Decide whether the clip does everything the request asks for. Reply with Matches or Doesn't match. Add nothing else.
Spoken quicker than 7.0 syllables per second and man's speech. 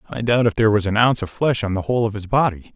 Matches